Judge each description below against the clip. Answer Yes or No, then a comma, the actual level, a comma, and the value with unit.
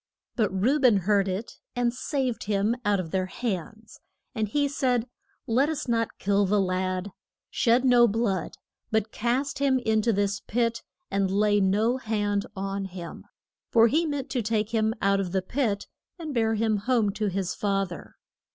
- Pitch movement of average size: Yes, average, 3.4 semitones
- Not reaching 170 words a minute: No, average, 180 wpm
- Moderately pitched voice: No, high, 215 Hz